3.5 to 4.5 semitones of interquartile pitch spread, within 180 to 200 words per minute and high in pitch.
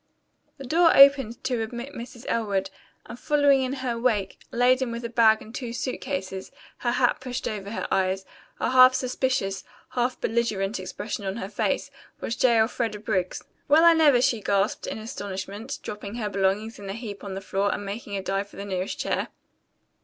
Yes: average, 4.1 semitones; average, 190 wpm; high, 225 Hz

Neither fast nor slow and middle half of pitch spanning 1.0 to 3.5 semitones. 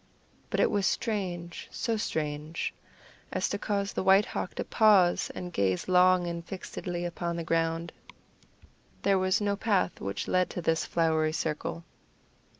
Yes: average, 150 wpm; average, 2.8 semitones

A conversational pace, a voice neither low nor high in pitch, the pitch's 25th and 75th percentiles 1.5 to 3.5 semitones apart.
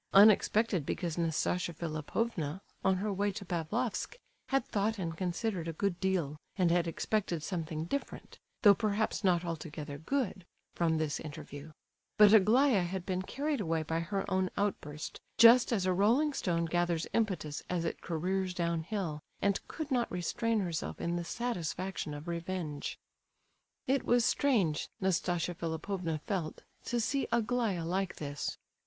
No: average, 150 wpm; medium, 180 Hz; average, 4.3 semitones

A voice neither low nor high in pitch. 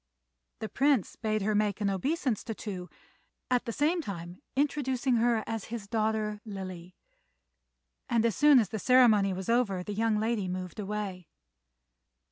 No: high, 215 Hz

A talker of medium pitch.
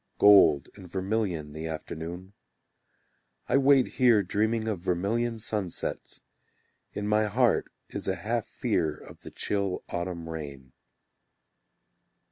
No: very low, 95 Hz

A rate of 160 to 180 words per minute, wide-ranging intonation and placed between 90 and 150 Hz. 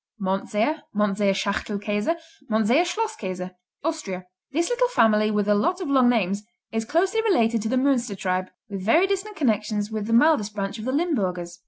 No: average, 170 wpm; wide, 7.6 semitones; high, 220 Hz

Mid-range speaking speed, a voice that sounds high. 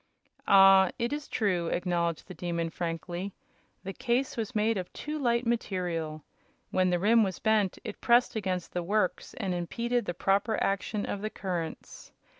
Yes: average, 165 wpm; high, 195 Hz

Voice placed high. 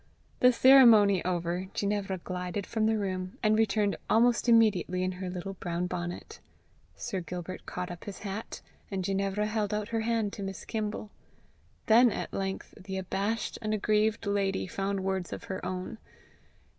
Yes: high, 200 Hz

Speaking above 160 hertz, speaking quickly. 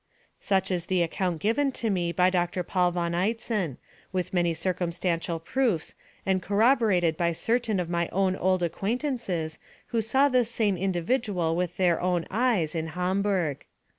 No: medium, 185 Hz; average, 155 wpm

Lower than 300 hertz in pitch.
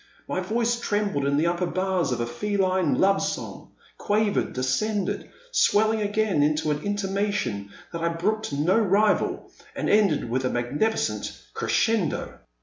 Yes: high, 190 Hz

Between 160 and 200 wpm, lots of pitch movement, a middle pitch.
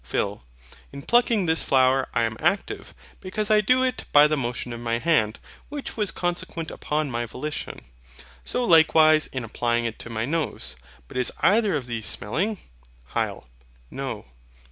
Yes: average, 165 wpm; wide, 8.1 semitones; medium, 150 Hz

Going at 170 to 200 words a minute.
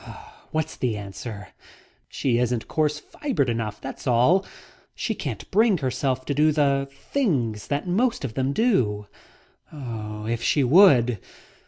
No: slow, 135 wpm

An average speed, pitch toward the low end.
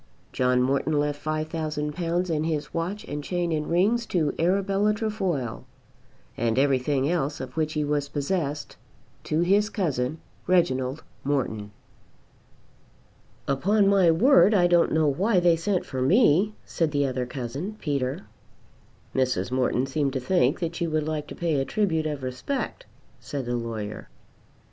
No: average, 150 wpm; medium, 155 Hz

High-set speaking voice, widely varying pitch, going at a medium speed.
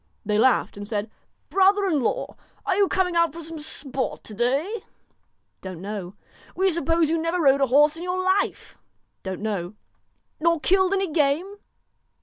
Yes: very high, 315 Hz; wide, 7.4 semitones; average, 185 wpm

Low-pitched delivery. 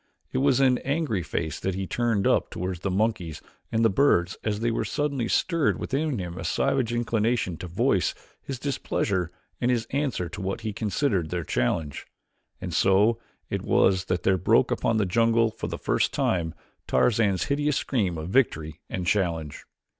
Yes: low, 105 Hz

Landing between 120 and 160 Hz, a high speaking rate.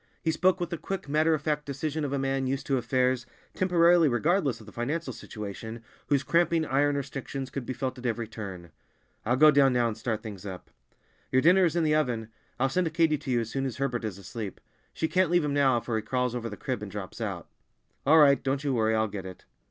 Yes: low, 135 Hz; fast, 235 wpm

